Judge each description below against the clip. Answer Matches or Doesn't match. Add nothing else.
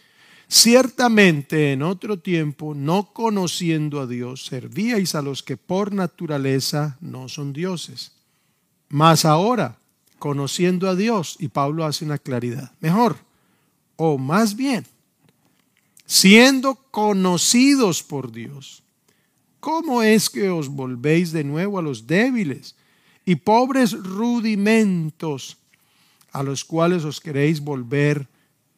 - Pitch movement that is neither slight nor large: Doesn't match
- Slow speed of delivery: Matches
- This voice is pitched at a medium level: Matches